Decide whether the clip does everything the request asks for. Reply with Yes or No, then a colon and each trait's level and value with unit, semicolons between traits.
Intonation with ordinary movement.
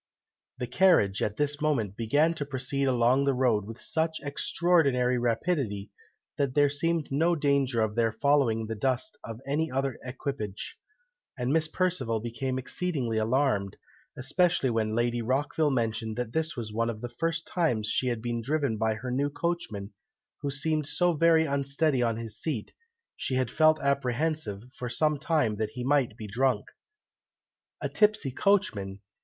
Yes: average, 5.0 semitones